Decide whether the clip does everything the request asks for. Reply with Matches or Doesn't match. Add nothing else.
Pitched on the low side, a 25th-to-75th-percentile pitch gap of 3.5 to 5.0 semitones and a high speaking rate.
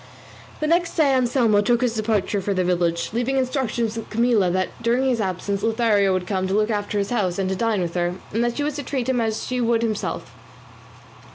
Doesn't match